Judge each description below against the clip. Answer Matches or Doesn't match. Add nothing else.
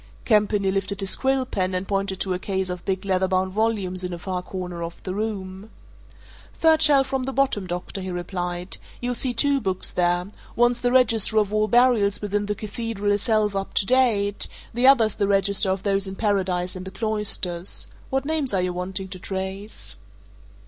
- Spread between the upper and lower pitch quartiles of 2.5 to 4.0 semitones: Matches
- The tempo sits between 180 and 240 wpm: Matches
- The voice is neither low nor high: Doesn't match